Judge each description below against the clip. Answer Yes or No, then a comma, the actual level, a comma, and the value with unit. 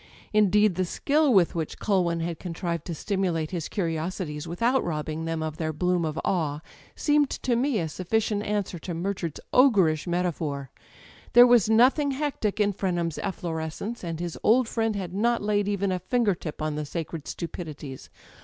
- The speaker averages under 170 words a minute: No, average, 175 wpm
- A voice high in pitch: No, medium, 180 Hz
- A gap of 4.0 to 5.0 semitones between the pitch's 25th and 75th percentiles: Yes, average, 4.5 semitones